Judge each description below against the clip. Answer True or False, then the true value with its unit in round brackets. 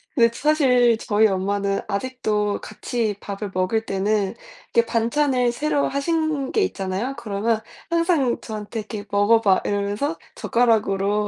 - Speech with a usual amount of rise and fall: True (4.2 semitones)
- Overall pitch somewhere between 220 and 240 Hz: True (225 Hz)